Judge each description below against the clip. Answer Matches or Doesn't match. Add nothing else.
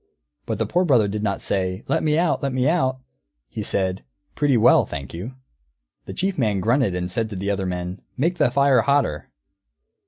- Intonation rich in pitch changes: Matches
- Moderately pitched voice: Doesn't match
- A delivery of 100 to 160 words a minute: Doesn't match